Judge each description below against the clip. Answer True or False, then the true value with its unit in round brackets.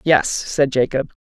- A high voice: False (140 Hz)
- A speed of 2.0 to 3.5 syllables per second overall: False (3.9 syllables/s)